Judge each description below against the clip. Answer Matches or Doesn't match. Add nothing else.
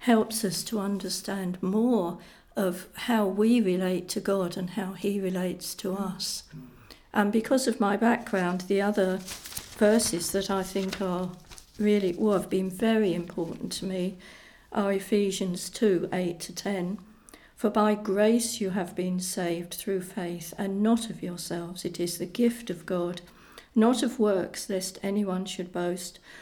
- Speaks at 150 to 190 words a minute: Matches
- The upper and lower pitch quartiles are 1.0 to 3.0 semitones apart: Matches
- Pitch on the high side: Matches